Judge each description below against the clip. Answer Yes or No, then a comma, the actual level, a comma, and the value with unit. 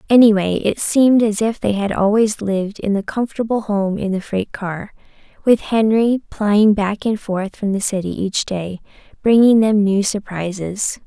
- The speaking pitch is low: No, high, 205 Hz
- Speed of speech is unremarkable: Yes, average, 175 wpm